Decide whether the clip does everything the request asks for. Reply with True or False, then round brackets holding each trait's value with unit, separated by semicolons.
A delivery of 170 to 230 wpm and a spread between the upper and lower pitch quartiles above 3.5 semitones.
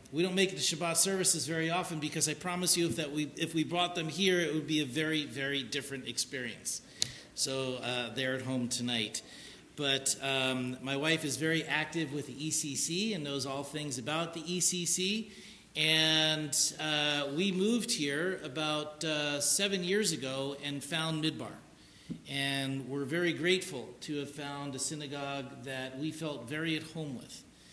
False (175 wpm; 3.2 semitones)